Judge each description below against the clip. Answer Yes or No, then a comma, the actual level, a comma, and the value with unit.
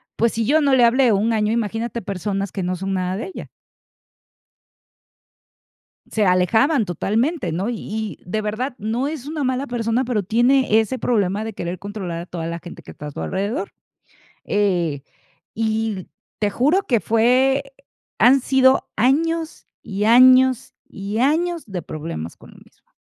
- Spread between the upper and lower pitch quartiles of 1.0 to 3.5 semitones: No, average, 4.9 semitones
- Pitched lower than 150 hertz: No, high, 220 Hz